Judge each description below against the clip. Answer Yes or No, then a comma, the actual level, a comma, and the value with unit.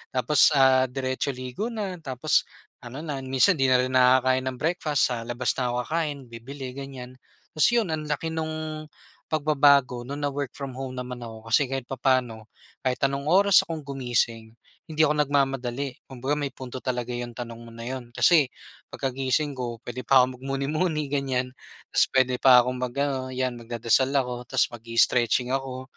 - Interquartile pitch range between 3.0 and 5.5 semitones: No, narrow, 2.5 semitones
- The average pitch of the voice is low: Yes, low, 130 Hz